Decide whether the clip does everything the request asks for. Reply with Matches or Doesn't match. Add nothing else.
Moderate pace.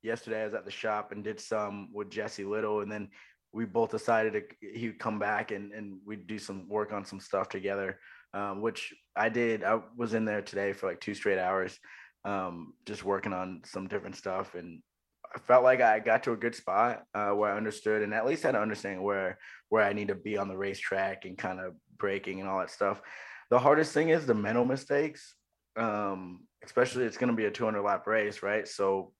Doesn't match